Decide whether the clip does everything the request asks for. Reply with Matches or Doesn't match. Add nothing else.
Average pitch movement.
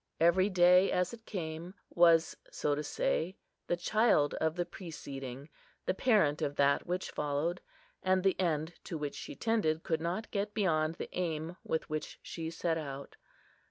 Matches